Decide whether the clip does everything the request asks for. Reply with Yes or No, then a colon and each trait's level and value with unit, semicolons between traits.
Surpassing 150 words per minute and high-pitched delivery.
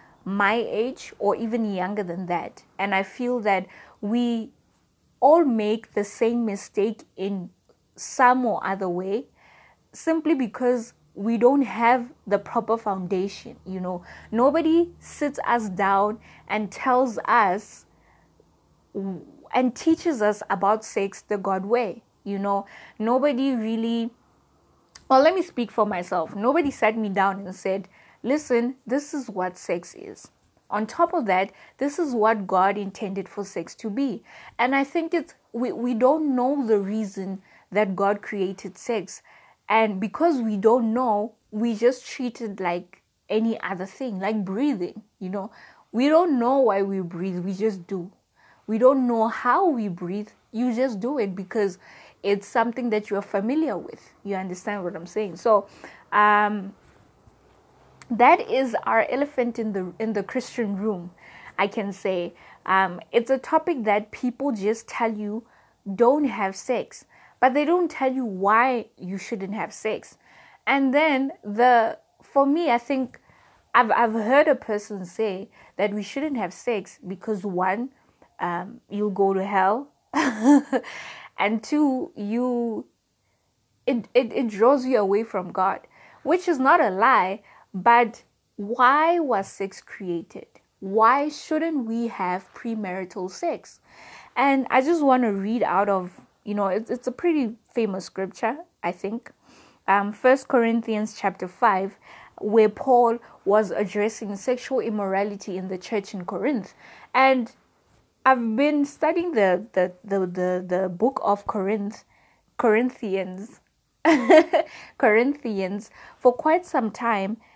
No: average, 145 wpm; high, 220 Hz